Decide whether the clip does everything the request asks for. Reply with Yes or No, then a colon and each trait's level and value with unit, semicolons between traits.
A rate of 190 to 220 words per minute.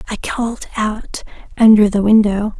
No: average, 140 wpm